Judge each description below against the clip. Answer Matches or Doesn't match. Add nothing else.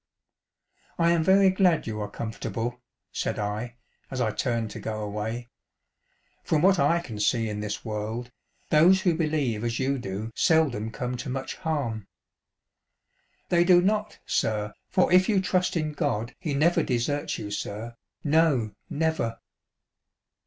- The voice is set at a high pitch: Doesn't match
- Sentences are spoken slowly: Doesn't match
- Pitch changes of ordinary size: Doesn't match